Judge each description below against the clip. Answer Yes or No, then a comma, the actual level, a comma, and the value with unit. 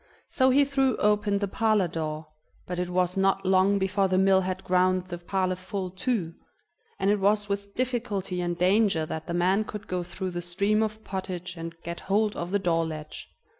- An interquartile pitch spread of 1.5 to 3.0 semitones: Yes, narrow, 2.5 semitones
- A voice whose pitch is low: No, high, 190 Hz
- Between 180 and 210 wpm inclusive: Yes, average, 200 wpm